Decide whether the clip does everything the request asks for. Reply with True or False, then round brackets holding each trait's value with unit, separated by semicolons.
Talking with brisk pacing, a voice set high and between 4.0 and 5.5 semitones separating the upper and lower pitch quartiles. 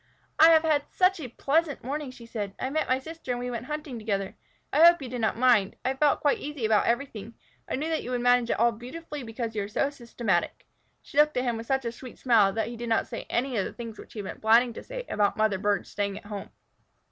True (265 wpm; 245 Hz; 4.3 semitones)